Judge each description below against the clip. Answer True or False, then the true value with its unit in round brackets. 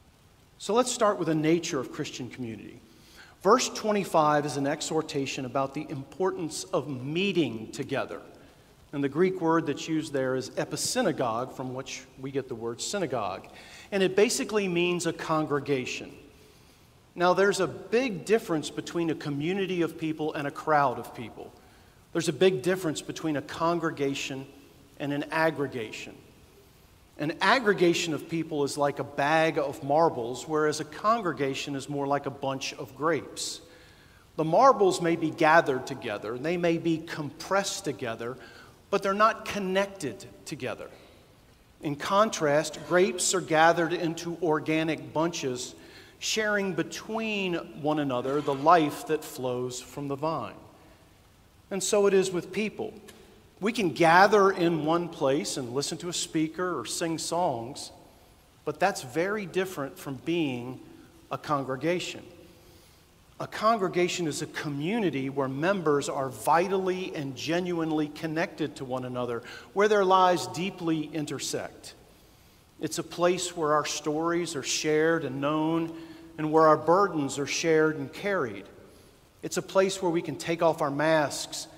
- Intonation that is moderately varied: True (3.9 semitones)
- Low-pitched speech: False (155 Hz)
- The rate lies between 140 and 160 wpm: True (145 wpm)